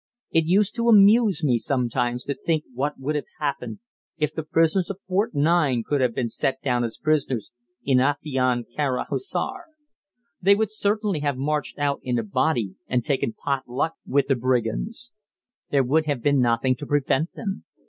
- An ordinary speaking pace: Yes, average, 180 wpm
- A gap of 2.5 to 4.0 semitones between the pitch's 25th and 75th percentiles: No, average, 4.4 semitones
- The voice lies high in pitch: No, medium, 145 Hz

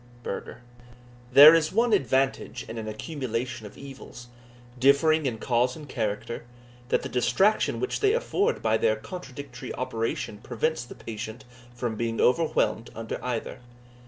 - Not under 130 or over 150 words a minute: Yes, average, 140 wpm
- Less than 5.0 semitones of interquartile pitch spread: No, average, 5.3 semitones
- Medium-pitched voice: No, low, 125 Hz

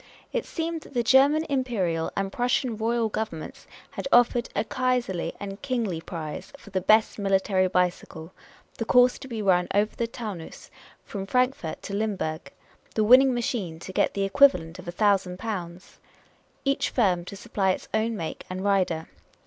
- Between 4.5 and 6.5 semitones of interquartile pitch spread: Yes, average, 5.0 semitones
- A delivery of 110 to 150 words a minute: No, average, 170 wpm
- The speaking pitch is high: Yes, high, 205 Hz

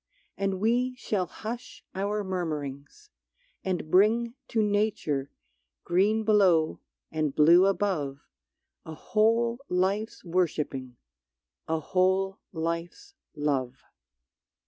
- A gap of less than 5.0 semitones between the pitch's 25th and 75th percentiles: No, average, 5.3 semitones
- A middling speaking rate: No, slow, 95 wpm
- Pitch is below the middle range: No, medium, 185 Hz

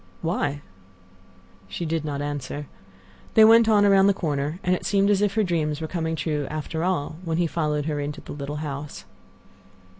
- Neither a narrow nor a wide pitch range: Yes, average, 4.1 semitones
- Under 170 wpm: No, average, 185 wpm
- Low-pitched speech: No, medium, 160 Hz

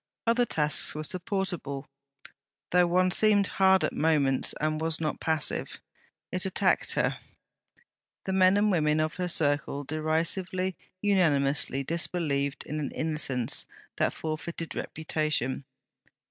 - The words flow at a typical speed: No, slow, 120 wpm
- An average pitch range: Yes, average, 3.5 semitones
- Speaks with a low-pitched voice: No, medium, 160 Hz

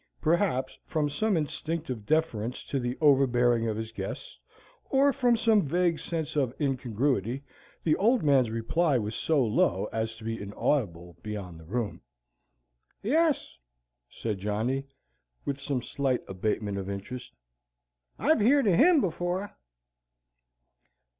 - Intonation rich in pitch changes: Yes, wide, 7.1 semitones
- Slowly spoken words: Yes, slow, 130 wpm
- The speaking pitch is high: No, low, 135 Hz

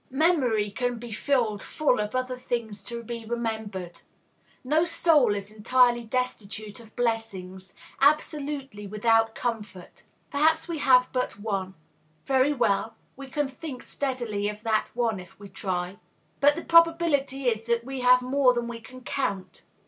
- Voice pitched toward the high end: Yes, high, 240 Hz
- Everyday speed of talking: Yes, average, 150 wpm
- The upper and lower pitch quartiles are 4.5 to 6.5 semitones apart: No, average, 4.1 semitones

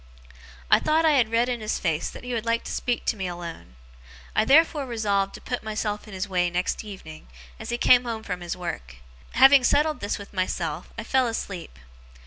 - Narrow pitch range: No, average, 5.2 semitones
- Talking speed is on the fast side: Yes, fast, 210 wpm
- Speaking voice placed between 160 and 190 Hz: No, high, 215 Hz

